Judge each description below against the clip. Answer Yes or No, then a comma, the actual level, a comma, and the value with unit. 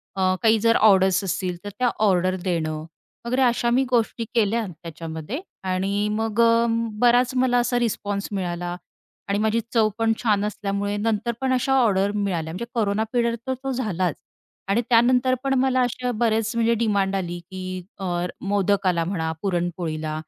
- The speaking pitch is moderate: No, high, 205 Hz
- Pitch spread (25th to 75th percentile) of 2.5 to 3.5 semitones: No, average, 4.1 semitones